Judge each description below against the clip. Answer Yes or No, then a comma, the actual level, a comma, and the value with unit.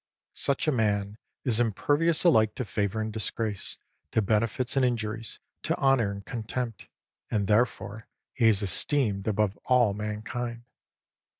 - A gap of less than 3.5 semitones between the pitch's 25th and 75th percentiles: Yes, average, 2.8 semitones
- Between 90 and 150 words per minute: Yes, slow, 135 wpm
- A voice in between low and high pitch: No, low, 110 Hz